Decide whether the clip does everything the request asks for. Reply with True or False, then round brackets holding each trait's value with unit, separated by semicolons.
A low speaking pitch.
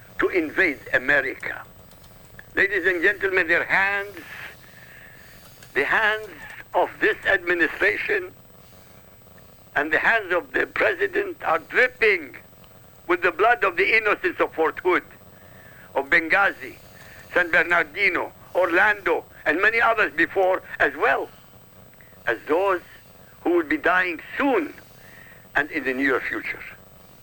False (360 Hz)